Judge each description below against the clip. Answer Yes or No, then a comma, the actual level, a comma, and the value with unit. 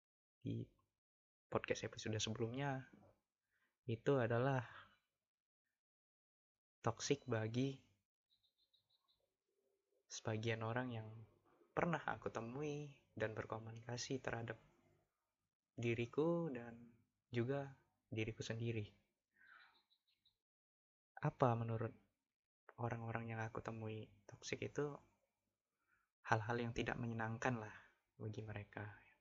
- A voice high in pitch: No, low, 115 Hz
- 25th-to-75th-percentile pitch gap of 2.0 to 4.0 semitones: Yes, narrow, 2.5 semitones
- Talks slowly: Yes, slow, 75 wpm